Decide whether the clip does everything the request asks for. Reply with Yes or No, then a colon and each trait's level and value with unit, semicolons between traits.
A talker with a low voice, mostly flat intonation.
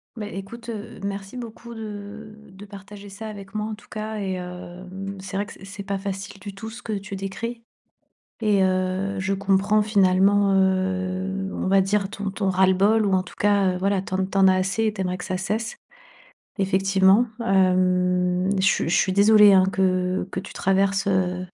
No: high, 195 Hz; narrow, 1.6 semitones